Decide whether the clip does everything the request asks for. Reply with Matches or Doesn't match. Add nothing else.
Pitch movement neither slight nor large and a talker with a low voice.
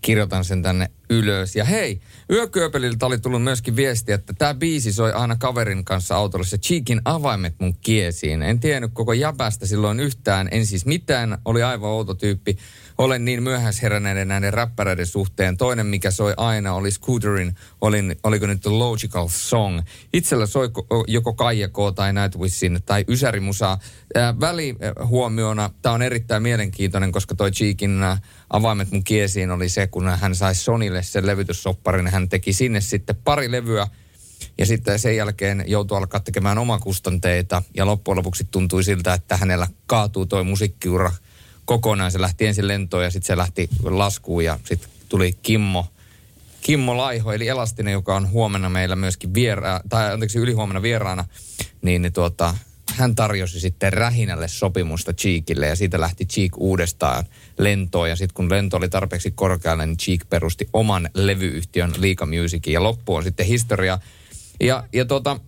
Matches